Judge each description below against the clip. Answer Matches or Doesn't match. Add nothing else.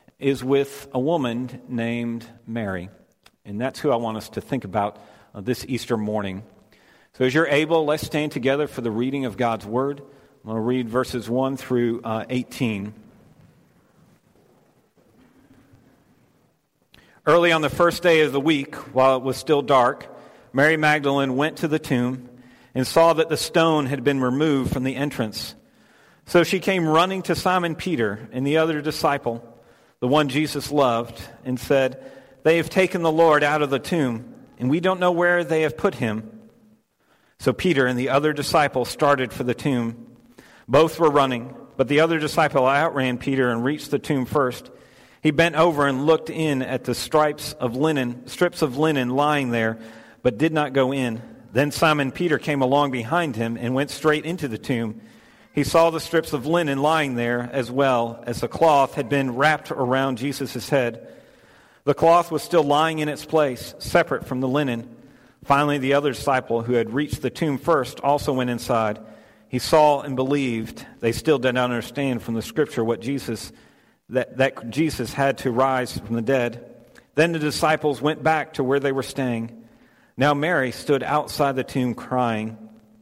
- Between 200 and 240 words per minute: Doesn't match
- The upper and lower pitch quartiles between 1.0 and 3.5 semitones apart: Doesn't match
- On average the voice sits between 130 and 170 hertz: Matches